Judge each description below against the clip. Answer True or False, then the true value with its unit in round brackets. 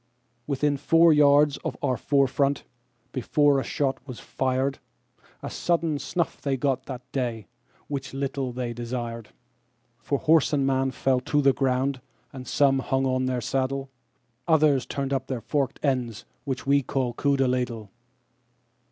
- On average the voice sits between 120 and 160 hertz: True (135 Hz)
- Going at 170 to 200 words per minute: False (145 wpm)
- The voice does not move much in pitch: True (1.9 semitones)